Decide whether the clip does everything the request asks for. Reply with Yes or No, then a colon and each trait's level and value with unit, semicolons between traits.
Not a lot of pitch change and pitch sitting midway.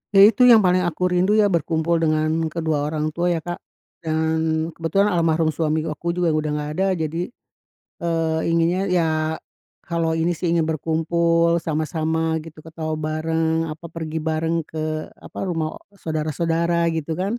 Yes: narrow, 1.3 semitones; medium, 160 Hz